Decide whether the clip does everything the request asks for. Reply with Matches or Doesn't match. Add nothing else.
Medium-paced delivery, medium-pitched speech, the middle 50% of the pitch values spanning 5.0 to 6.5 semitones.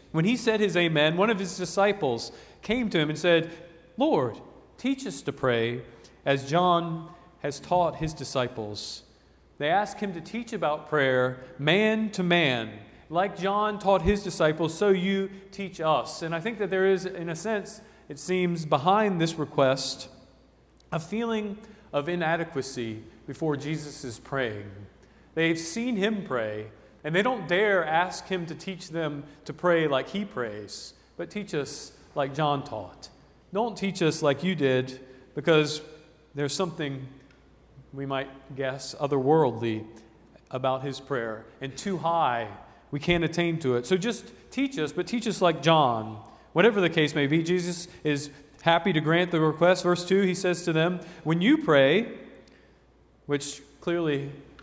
Matches